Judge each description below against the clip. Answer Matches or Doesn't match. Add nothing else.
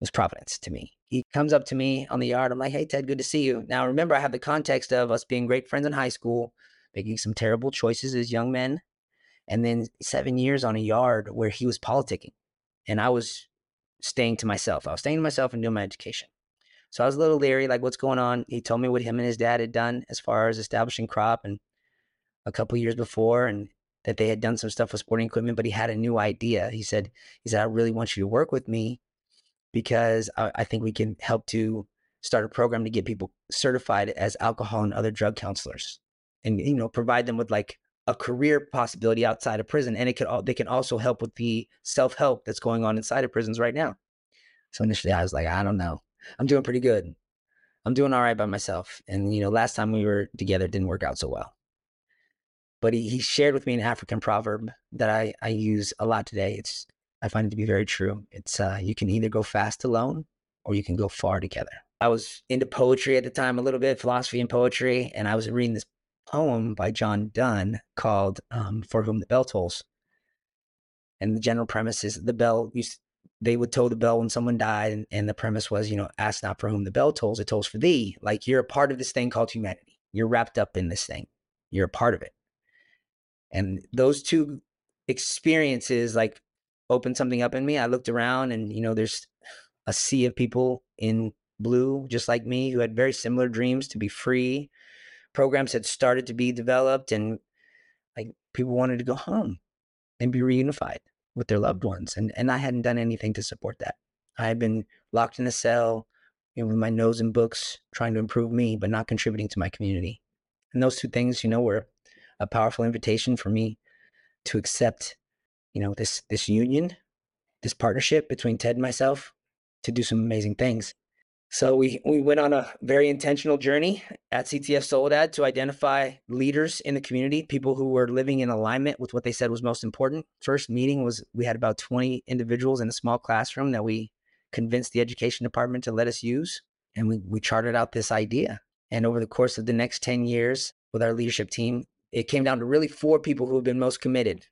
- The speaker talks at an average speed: Doesn't match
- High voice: Doesn't match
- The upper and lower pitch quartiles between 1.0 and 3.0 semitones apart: Matches